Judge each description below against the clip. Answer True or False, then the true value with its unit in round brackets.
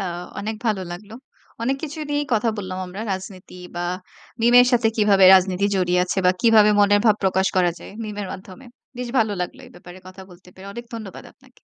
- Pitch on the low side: False (200 Hz)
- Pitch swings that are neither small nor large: True (3.1 semitones)